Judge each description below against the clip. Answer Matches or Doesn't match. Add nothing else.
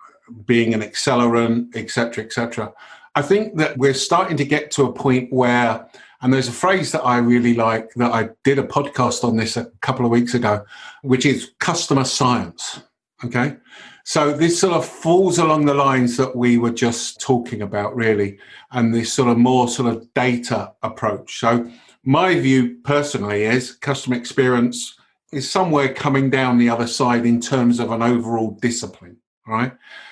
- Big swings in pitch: Doesn't match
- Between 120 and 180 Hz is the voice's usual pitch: Matches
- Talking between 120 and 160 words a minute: Doesn't match